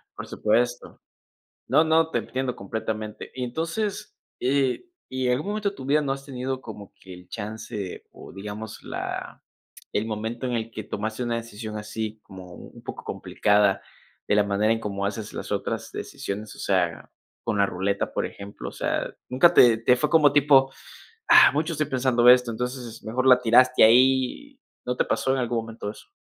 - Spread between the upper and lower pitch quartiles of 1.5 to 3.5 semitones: No, average, 4.0 semitones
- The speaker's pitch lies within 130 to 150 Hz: No, low, 120 Hz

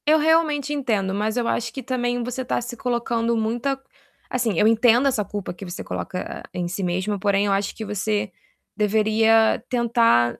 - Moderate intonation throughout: Yes, average, 3.2 semitones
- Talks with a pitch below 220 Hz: No, high, 225 Hz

